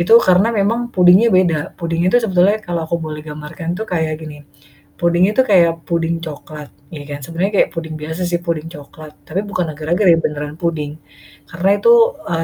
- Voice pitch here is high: No, medium, 170 Hz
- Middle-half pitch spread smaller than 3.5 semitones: Yes, average, 2.7 semitones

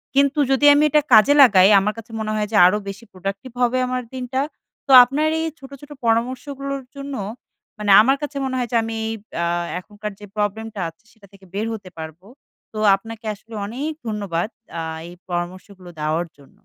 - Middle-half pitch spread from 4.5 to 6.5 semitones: Yes, average, 4.8 semitones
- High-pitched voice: Yes, high, 220 Hz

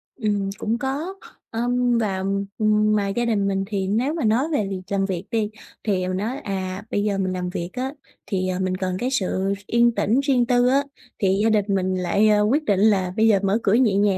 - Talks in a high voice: Yes, high, 210 Hz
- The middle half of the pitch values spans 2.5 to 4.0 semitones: Yes, average, 3.6 semitones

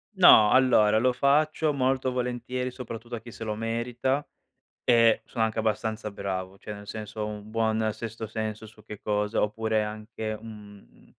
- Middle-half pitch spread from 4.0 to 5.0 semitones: No, narrow, 2.4 semitones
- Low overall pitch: Yes, low, 110 Hz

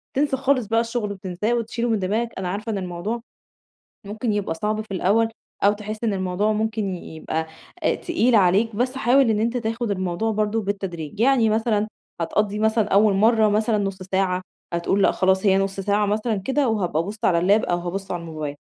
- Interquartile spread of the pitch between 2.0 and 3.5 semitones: Yes, average, 2.9 semitones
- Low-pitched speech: No, high, 210 Hz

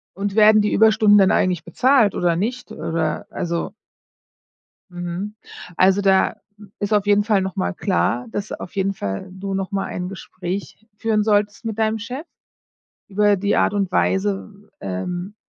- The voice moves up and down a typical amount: No, narrow, 2.3 semitones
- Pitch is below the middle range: No, high, 200 Hz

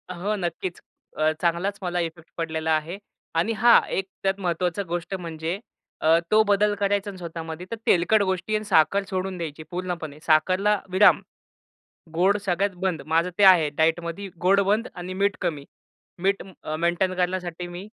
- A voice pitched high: No, medium, 180 Hz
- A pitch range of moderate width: Yes, average, 3.0 semitones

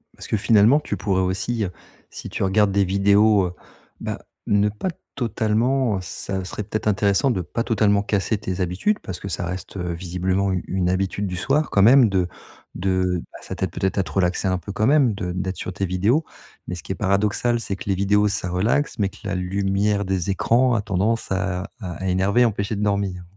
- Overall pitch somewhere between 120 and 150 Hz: No, low, 100 Hz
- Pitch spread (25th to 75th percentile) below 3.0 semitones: Yes, narrow, 2.4 semitones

